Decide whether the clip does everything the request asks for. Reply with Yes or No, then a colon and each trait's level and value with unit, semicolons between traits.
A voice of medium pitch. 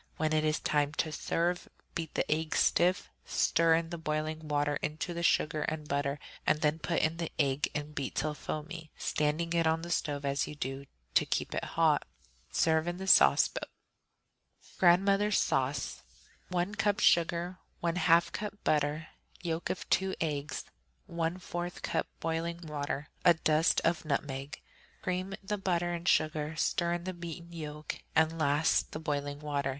Yes: medium, 160 Hz